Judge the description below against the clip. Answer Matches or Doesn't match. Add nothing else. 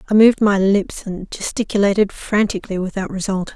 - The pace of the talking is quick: Doesn't match